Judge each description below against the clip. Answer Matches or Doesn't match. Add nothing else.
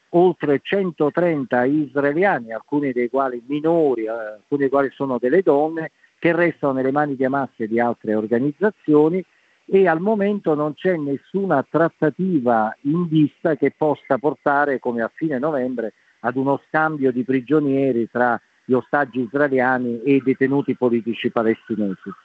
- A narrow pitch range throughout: Doesn't match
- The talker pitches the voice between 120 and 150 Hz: Matches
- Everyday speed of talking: Matches